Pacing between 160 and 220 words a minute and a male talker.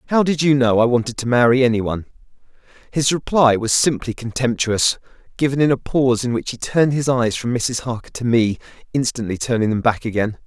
Yes: average, 200 wpm; male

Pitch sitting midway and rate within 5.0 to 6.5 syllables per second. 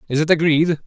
Yes: medium, 160 Hz; 6.3 syllables/s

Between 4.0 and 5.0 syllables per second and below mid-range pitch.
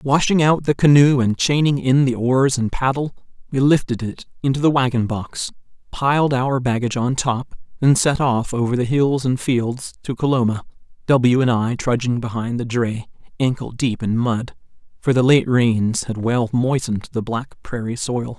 Yes: 4.7 syllables/s; low, 125 Hz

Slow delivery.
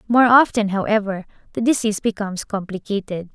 Yes: slow, 125 wpm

